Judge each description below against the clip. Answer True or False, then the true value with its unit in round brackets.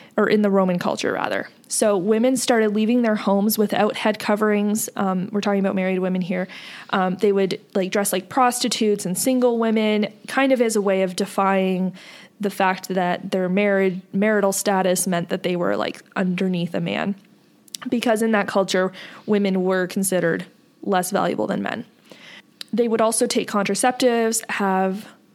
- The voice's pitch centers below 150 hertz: False (205 Hz)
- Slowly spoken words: False (170 wpm)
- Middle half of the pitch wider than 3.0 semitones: False (2.7 semitones)